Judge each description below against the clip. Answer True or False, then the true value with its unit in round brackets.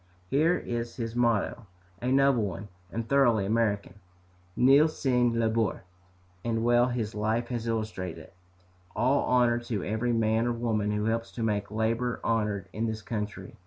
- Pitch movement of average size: False (2.0 semitones)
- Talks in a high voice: False (115 Hz)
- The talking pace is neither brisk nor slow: True (160 wpm)